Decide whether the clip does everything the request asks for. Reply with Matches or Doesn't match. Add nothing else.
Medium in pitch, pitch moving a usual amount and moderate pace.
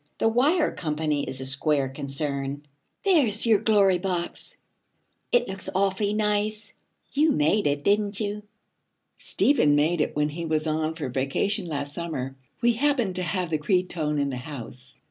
Doesn't match